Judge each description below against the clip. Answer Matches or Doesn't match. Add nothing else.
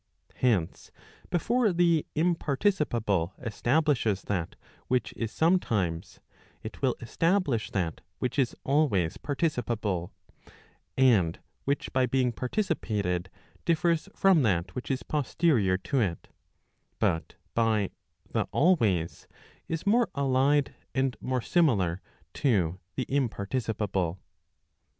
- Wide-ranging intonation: Matches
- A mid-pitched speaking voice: Doesn't match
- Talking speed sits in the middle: Doesn't match